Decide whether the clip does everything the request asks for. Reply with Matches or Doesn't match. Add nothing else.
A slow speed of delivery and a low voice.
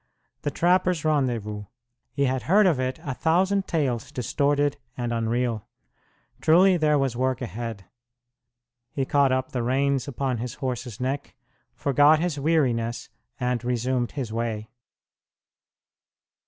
Matches